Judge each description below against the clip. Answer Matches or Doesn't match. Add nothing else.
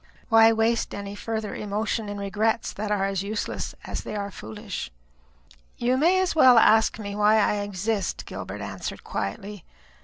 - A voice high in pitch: Matches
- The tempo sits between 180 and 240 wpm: Doesn't match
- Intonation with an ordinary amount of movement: Doesn't match